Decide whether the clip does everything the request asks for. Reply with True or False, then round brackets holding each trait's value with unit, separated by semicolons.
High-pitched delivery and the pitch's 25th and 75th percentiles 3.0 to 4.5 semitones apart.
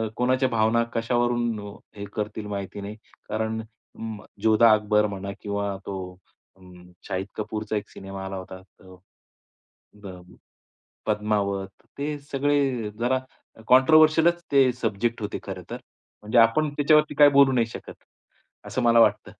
False (110 Hz; 4.0 semitones)